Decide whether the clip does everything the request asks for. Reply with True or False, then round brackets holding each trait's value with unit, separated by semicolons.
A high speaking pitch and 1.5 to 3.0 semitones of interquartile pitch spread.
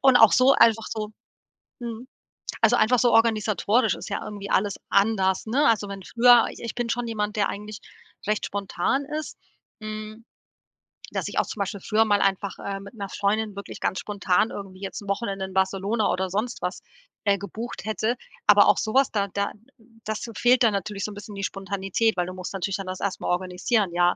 True (205 Hz; 2.4 semitones)